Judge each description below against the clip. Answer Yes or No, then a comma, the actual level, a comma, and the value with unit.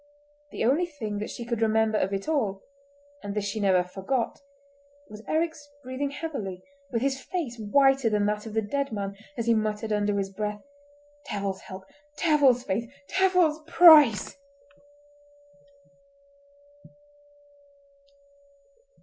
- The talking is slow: Yes, slow, 125 wpm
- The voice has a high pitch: Yes, high, 235 Hz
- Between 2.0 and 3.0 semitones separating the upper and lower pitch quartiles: No, wide, 5.4 semitones